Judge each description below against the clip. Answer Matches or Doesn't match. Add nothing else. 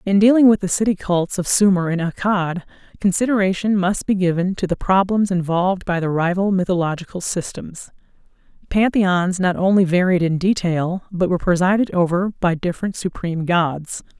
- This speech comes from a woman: Matches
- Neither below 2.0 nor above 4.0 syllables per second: Doesn't match